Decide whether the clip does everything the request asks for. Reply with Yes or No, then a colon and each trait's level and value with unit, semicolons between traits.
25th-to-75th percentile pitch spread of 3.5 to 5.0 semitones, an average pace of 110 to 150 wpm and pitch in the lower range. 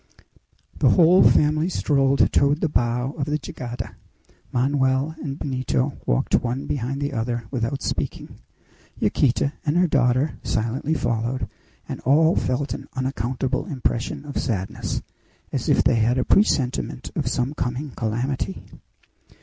No: average, 2.9 semitones; slow, 135 wpm; low, 130 Hz